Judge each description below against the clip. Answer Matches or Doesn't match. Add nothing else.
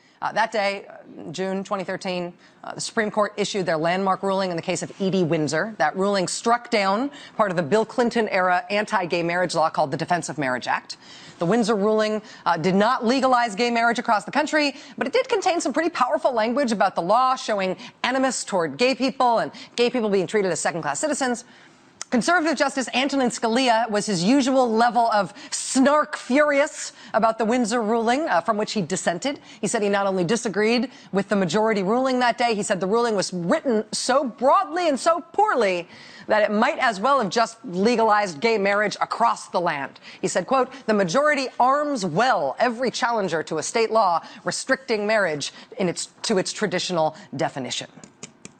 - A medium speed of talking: Matches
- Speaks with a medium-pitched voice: Doesn't match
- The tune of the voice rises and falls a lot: Doesn't match